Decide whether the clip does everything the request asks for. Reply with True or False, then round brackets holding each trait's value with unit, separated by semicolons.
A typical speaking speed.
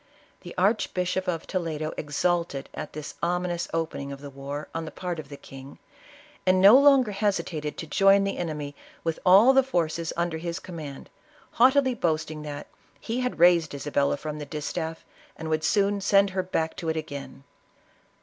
True (180 wpm)